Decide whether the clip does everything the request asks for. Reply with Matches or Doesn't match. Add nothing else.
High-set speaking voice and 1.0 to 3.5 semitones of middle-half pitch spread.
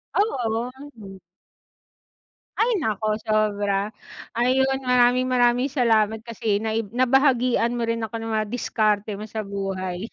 Matches